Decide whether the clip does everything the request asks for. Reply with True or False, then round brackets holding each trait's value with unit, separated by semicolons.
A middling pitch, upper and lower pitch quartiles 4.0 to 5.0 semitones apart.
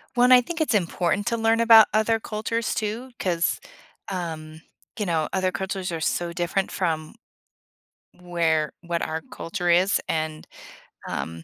True (180 Hz; 4.7 semitones)